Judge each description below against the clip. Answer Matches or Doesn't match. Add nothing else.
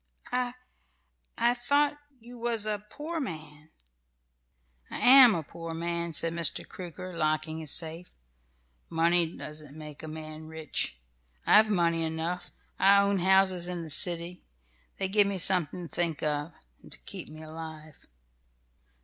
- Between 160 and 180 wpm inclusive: Doesn't match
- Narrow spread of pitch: Doesn't match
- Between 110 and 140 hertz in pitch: Doesn't match